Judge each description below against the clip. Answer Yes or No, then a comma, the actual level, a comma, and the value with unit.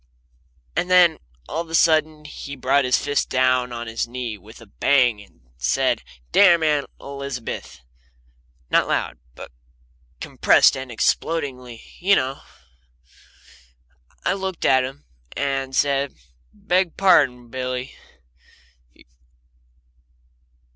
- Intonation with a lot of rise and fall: No, average, 3.9 semitones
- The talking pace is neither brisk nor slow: No, slow, 115 wpm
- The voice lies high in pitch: No, low, 135 Hz